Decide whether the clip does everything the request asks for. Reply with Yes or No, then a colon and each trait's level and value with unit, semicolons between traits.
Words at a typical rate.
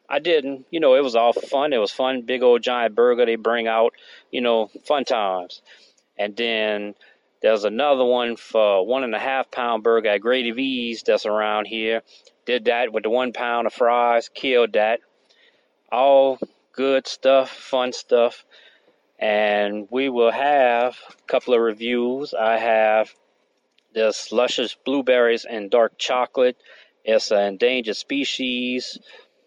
Yes: average, 155 wpm